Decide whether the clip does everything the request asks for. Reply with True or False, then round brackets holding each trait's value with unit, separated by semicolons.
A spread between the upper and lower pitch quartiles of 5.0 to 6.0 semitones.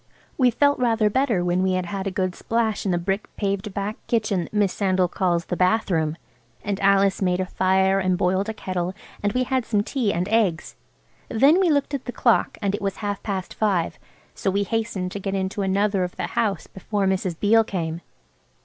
False (2.8 semitones)